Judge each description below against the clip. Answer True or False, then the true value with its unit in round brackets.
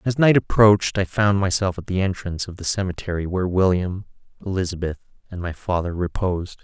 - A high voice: False (95 Hz)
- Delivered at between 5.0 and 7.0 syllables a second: True (6.0 syllables/s)